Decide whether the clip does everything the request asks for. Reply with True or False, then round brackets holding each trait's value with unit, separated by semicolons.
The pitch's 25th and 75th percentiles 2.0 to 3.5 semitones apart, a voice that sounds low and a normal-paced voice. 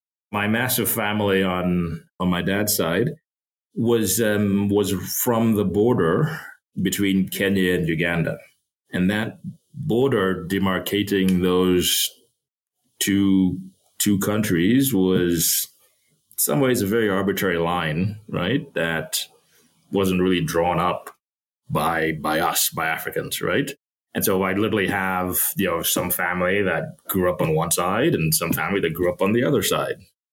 False (2.4 semitones; 95 Hz; 140 wpm)